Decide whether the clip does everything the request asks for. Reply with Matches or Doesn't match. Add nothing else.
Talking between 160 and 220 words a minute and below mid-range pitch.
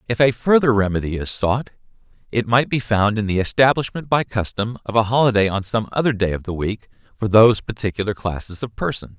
Matches